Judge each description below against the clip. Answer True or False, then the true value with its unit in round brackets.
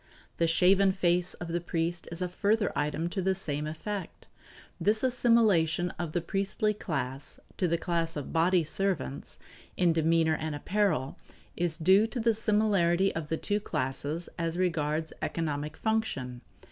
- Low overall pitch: False (170 Hz)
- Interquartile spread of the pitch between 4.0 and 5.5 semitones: False (3.6 semitones)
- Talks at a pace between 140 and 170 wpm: True (155 wpm)